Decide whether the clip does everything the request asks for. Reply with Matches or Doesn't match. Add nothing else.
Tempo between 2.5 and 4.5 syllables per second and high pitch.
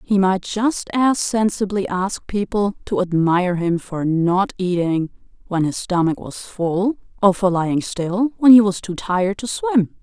Matches